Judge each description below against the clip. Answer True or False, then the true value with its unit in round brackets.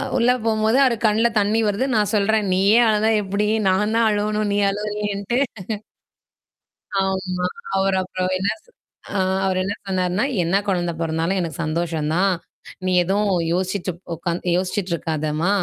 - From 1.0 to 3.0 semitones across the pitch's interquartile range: True (2.6 semitones)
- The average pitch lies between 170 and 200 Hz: True (195 Hz)